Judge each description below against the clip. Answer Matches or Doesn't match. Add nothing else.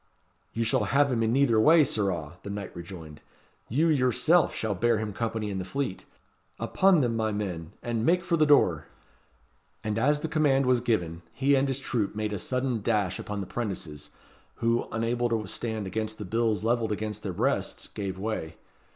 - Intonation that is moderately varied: Matches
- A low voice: Matches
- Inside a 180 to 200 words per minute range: Matches